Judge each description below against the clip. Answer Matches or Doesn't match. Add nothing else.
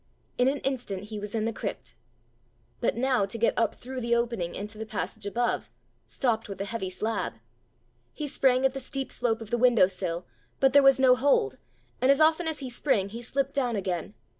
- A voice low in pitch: Doesn't match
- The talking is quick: Matches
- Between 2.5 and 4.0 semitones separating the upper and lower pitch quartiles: Doesn't match